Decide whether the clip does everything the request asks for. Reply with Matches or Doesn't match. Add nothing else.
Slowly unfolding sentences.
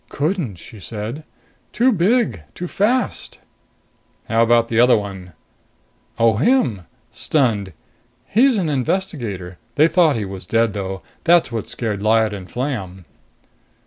Matches